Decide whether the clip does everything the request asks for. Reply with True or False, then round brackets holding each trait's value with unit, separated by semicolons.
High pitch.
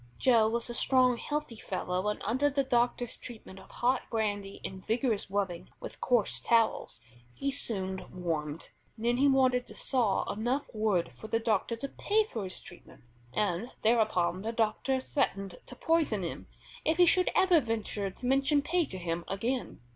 True (225 Hz)